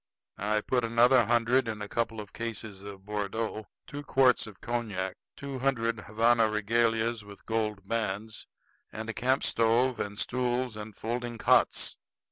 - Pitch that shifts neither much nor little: No, narrow, 2.2 semitones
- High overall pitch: No, low, 115 Hz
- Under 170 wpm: Yes, average, 150 wpm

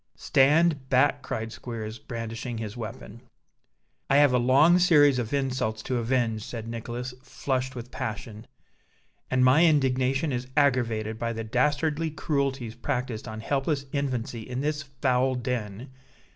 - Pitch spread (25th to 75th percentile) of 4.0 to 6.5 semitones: No, average, 3.3 semitones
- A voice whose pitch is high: No, low, 125 Hz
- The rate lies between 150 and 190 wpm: No, average, 140 wpm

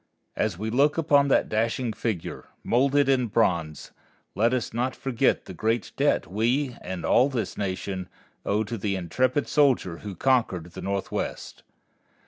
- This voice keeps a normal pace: Yes, average, 150 wpm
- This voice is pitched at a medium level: No, low, 115 Hz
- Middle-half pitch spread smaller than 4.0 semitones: No, average, 5.2 semitones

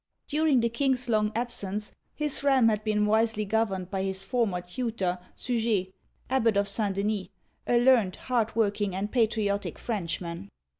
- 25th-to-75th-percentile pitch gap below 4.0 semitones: Yes, average, 3.3 semitones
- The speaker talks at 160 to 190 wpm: Yes, average, 165 wpm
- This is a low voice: No, high, 215 Hz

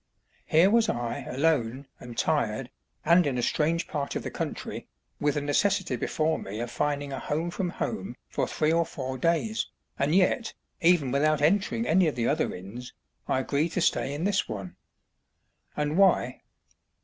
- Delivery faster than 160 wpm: Yes, average, 175 wpm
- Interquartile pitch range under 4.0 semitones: No, average, 4.6 semitones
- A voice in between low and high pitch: Yes, medium, 150 Hz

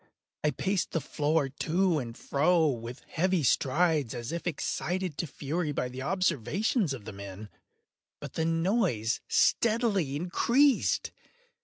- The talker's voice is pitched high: No, medium, 160 Hz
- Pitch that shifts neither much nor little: No, wide, 5.7 semitones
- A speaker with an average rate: No, slow, 130 wpm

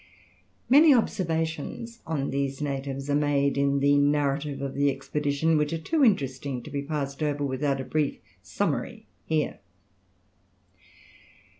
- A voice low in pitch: No, medium, 145 Hz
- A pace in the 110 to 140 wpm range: Yes, slow, 135 wpm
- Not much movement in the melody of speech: Yes, narrow, 2.2 semitones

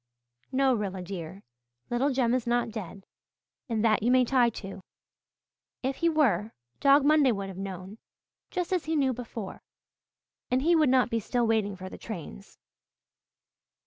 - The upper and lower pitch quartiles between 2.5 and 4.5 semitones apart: No, average, 5.0 semitones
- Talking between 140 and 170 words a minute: Yes, average, 160 wpm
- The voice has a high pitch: Yes, high, 235 Hz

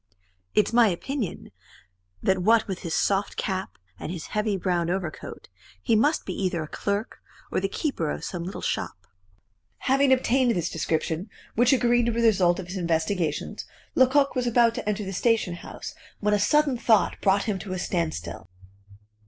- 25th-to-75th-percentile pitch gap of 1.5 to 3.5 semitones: No, average, 5.0 semitones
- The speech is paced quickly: No, average, 175 wpm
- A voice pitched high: Yes, high, 200 Hz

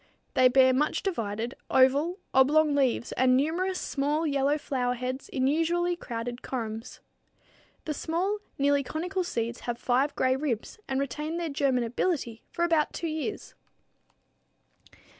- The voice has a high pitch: Yes, very high, 275 Hz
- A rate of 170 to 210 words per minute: No, slow, 135 wpm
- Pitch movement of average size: Yes, average, 4.1 semitones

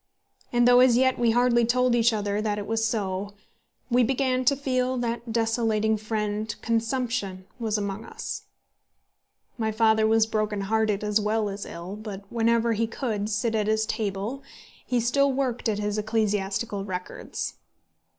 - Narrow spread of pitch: Yes, narrow, 2.3 semitones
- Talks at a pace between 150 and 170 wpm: Yes, average, 160 wpm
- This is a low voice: No, high, 220 Hz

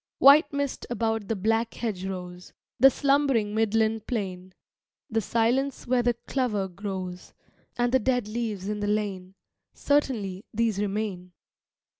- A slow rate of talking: Yes, slow, 130 wpm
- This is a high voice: Yes, high, 220 Hz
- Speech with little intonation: No, average, 3.8 semitones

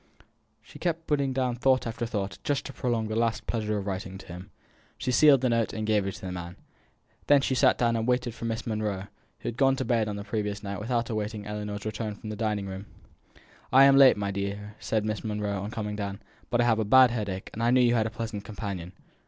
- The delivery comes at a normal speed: No, fast, 245 wpm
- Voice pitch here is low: Yes, low, 110 Hz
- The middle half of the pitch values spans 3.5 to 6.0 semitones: No, average, 2.9 semitones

